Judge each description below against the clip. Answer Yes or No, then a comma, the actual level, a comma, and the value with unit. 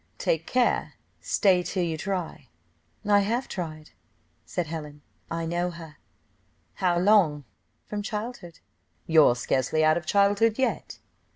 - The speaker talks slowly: Yes, slow, 125 wpm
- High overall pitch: No, medium, 175 Hz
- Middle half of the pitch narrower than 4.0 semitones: No, average, 4.5 semitones